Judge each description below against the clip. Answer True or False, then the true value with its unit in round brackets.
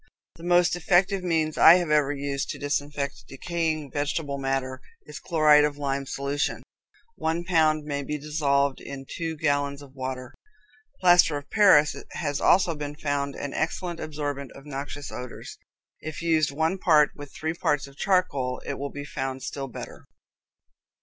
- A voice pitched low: False (145 Hz)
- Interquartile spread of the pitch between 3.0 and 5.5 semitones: False (2.5 semitones)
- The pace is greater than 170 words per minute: False (165 wpm)